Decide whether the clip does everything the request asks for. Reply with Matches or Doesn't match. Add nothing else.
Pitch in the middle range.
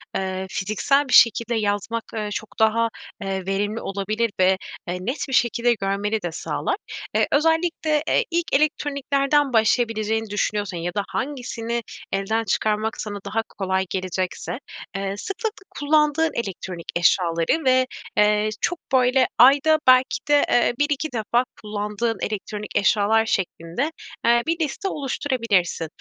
Doesn't match